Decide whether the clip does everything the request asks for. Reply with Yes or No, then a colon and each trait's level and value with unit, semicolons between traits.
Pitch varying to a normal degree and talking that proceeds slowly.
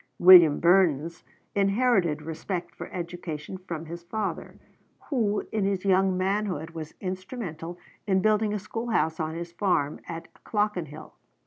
Yes: average, 3.6 semitones; slow, 130 wpm